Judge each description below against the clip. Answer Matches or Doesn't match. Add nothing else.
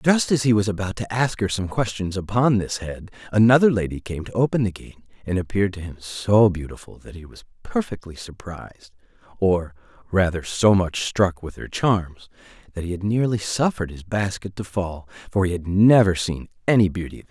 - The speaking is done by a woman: Doesn't match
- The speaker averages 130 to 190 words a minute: Doesn't match